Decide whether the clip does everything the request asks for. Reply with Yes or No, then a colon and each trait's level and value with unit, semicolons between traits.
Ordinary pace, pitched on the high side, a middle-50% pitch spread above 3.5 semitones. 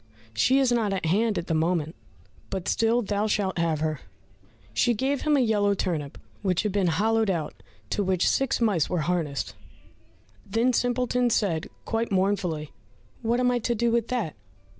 Yes: average, 175 wpm; high, 205 Hz; wide, 5.4 semitones